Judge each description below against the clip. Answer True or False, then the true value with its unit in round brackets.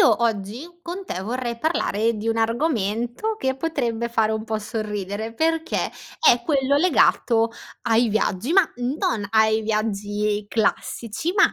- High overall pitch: True (230 Hz)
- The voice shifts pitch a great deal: False (4.5 semitones)